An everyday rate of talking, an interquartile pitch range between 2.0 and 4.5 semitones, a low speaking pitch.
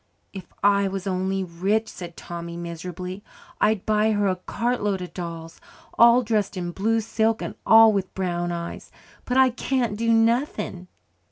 No: average, 160 wpm; average, 3.8 semitones; high, 195 Hz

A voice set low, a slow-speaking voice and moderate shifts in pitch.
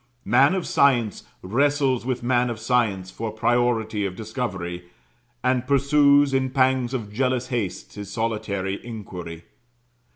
Yes: low, 120 Hz; slow, 130 wpm; average, 4.1 semitones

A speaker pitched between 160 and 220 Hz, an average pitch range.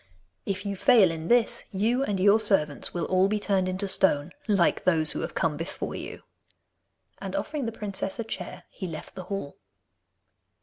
Yes: high, 190 Hz; average, 3.1 semitones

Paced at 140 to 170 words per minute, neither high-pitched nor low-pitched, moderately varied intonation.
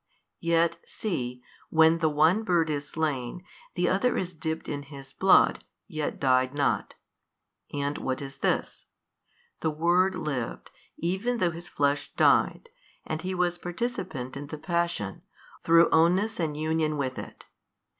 Yes: average, 145 wpm; medium, 160 Hz; average, 3.6 semitones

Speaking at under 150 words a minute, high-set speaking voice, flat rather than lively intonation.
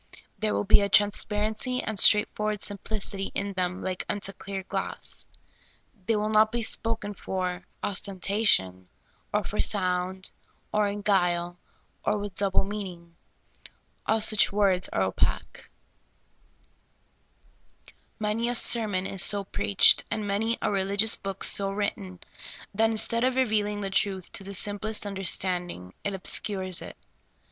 Yes: average, 140 wpm; high, 200 Hz; narrow, 2.1 semitones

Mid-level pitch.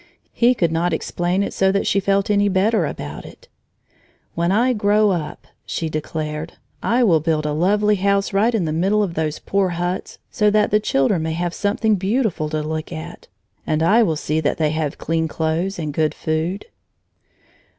Yes: medium, 175 Hz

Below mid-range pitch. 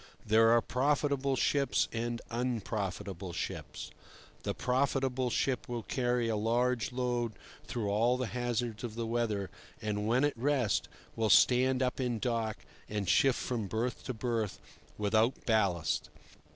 Yes: low, 120 Hz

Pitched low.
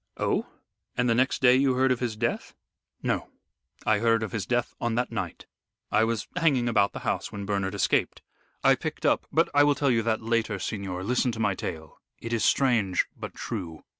Yes: low, 115 Hz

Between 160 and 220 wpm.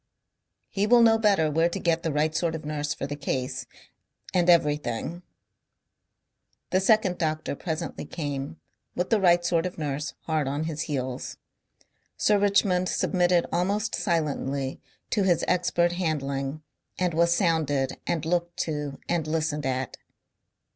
No: average, 145 wpm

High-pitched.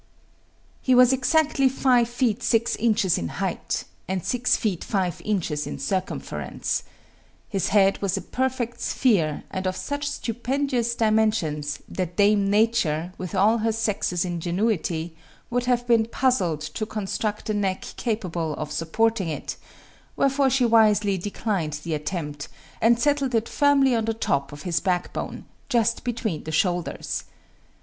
Yes: high, 210 Hz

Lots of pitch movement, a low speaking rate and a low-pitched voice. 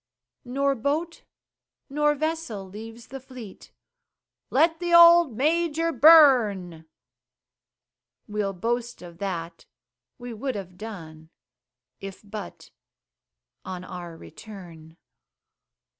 No: wide, 7.9 semitones; slow, 95 wpm; high, 225 Hz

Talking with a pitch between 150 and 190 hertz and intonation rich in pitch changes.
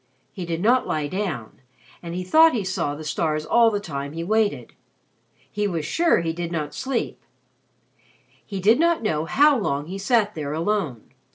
Yes: medium, 185 Hz; wide, 5.8 semitones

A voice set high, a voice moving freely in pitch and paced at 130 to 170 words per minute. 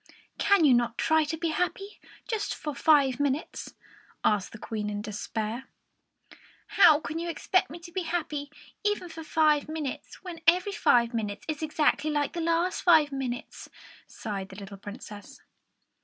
Yes: very high, 300 Hz; wide, 6.1 semitones; average, 160 wpm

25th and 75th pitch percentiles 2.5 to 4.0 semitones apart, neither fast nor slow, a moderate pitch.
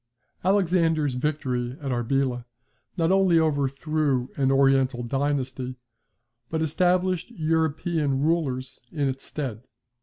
No: average, 3.6 semitones; slow, 100 wpm; medium, 145 Hz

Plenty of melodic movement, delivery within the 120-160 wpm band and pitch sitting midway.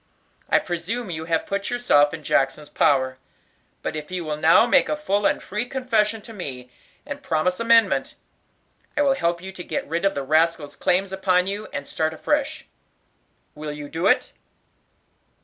No: wide, 5.7 semitones; average, 175 wpm; medium, 180 Hz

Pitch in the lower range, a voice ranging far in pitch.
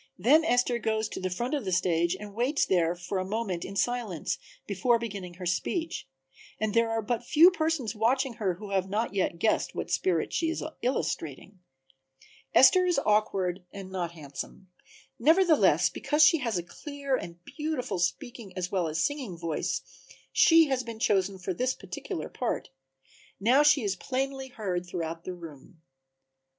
No: high, 215 Hz; wide, 6.3 semitones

